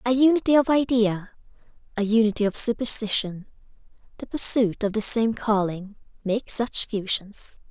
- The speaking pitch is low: No, high, 220 Hz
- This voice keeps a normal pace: No, slow, 130 wpm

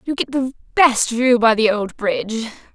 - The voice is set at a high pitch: Yes, high, 235 Hz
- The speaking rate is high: No, average, 195 wpm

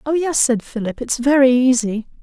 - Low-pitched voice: No, very high, 255 Hz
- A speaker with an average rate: Yes, average, 190 wpm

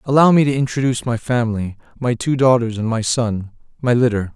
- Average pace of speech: Yes, average, 180 wpm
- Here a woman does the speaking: No, male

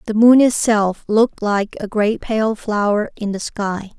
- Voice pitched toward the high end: Yes, high, 215 Hz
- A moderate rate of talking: Yes, average, 180 wpm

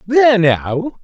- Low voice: No, high, 200 Hz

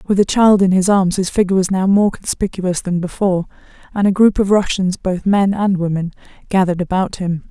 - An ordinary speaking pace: No, fast, 210 wpm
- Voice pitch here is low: No, high, 190 Hz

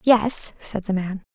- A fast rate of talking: No, average, 180 wpm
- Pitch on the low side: No, high, 205 Hz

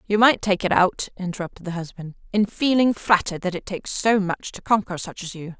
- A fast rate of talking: Yes, fast, 225 wpm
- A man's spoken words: No, female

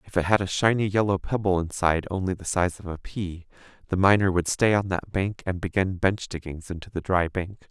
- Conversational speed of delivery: No, fast, 225 wpm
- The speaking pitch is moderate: No, very low, 95 Hz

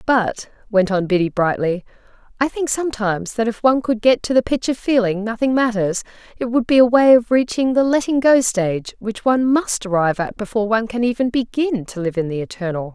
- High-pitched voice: Yes, high, 225 Hz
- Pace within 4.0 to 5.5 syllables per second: No, 5.8 syllables/s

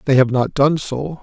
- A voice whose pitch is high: No, medium, 140 Hz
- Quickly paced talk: Yes, fast, 245 wpm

